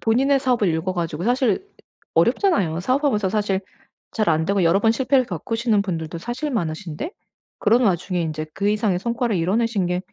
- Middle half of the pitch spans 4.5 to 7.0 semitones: Yes, wide, 5.5 semitones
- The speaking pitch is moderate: No, high, 205 Hz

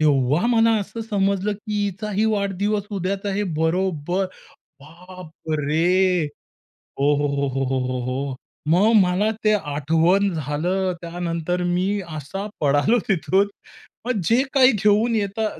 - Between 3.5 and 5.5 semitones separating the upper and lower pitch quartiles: Yes, average, 4.6 semitones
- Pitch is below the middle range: No, medium, 185 Hz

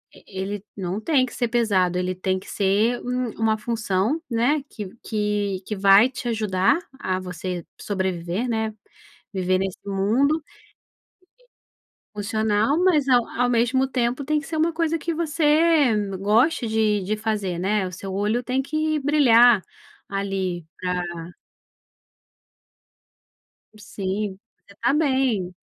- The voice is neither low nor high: No, high, 215 Hz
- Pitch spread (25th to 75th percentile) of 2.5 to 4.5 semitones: No, average, 5.2 semitones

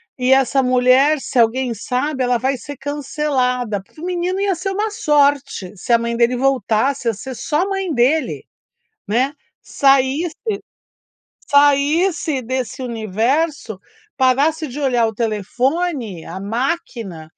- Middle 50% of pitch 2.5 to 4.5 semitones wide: Yes, average, 4.1 semitones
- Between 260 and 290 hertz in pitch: Yes, very high, 265 Hz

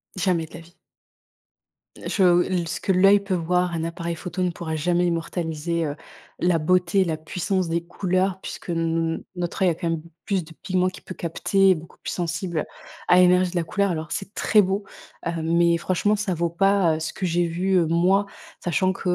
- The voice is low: No, medium, 175 Hz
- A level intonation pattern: Yes, narrow, 2.0 semitones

